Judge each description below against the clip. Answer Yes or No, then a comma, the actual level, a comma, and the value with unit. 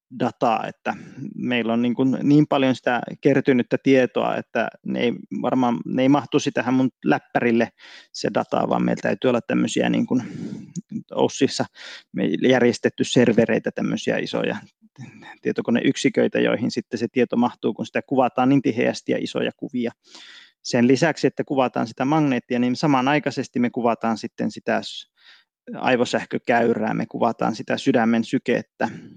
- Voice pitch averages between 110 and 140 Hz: Yes, low, 130 Hz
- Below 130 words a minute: No, average, 140 wpm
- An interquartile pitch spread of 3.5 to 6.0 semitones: No, average, 2.7 semitones